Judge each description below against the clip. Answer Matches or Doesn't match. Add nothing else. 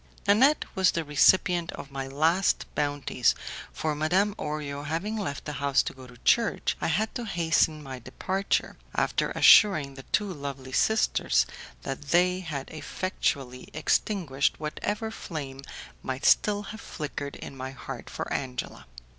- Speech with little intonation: Doesn't match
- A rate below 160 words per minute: Matches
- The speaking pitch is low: Doesn't match